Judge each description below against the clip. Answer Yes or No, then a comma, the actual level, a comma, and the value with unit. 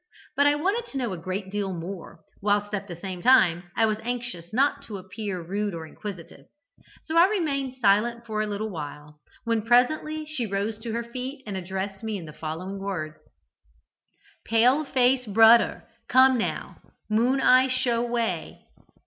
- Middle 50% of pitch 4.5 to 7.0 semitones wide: Yes, average, 4.8 semitones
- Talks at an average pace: Yes, average, 170 wpm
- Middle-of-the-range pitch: No, high, 220 Hz